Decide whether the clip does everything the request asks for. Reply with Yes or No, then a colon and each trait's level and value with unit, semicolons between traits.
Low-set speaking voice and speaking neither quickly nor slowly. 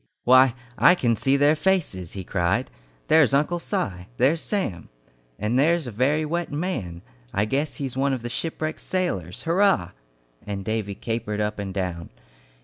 Yes: low, 125 Hz; average, 160 wpm